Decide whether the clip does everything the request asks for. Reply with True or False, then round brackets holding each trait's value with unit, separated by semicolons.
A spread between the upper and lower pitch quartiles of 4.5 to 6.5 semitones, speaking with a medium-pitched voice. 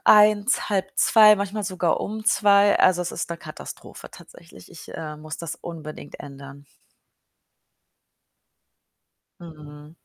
True (5.1 semitones; 175 Hz)